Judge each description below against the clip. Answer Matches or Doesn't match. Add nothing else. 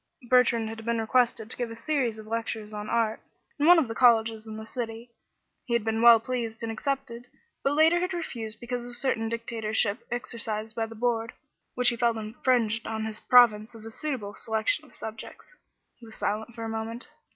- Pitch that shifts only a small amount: Matches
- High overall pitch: Matches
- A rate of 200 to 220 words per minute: Matches